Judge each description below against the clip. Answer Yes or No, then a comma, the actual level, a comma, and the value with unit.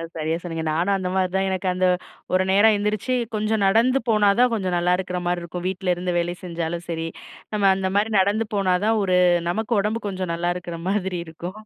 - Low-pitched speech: No, medium, 185 Hz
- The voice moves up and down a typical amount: Yes, average, 3.0 semitones